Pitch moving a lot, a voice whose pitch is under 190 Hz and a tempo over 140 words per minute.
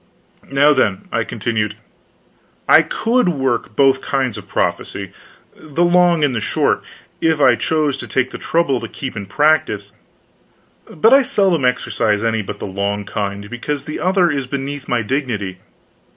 Yes: wide, 6.4 semitones; low, 135 Hz; average, 160 wpm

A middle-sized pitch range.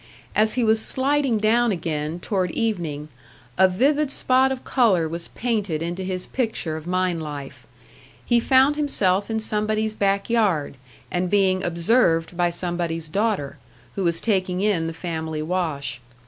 Yes: average, 5.0 semitones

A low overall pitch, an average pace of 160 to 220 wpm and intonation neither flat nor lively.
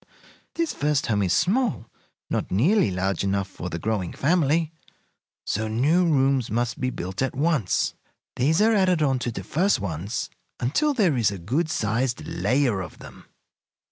No: low, 130 Hz; average, 165 wpm; wide, 7.9 semitones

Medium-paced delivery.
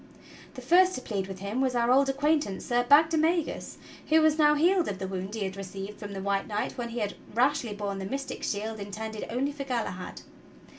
No: fast, 220 wpm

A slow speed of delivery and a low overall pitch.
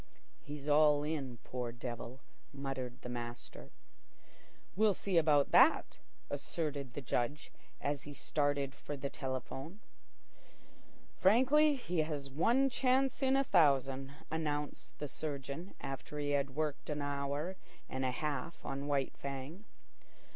No: slow, 130 wpm; medium, 145 Hz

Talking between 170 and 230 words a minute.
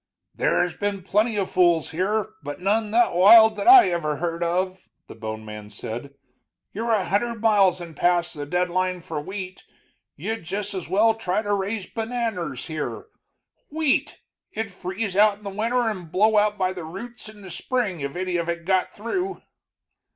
Yes: average, 180 wpm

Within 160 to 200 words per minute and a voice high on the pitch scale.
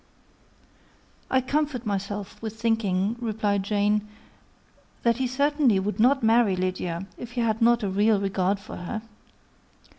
No: average, 140 wpm; high, 215 Hz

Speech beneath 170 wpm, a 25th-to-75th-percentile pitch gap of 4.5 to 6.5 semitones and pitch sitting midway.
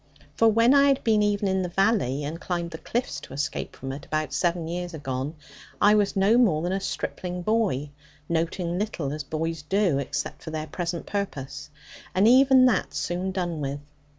No: average, 190 wpm; average, 5.2 semitones; medium, 175 Hz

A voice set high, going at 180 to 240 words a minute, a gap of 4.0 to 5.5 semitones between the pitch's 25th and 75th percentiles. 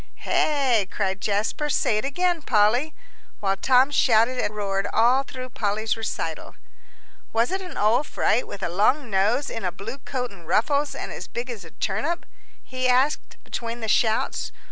No: high, 235 Hz; average, 170 wpm; average, 4.6 semitones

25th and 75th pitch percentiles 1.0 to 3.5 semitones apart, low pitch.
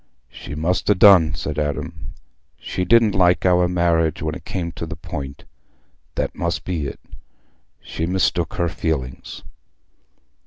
Yes: average, 2.8 semitones; very low, 85 Hz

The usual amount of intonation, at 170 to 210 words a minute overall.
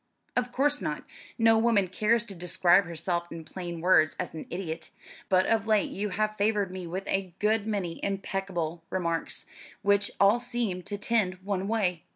Yes: average, 3.3 semitones; average, 175 wpm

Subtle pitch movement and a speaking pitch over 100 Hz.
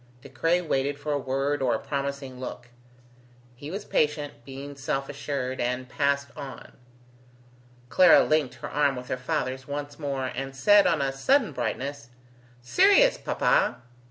Yes: narrow, 2.1 semitones; medium, 140 Hz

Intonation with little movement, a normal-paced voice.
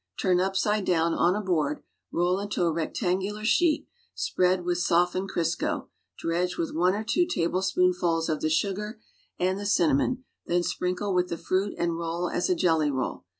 Yes: narrow, 2.3 semitones; average, 170 wpm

